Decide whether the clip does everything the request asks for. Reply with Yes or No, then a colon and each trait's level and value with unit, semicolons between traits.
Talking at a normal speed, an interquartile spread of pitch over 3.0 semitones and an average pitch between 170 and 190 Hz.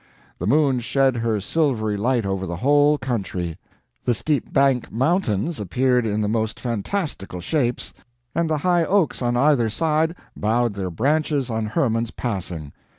No: average, 150 wpm; wide, 5.6 semitones; low, 120 Hz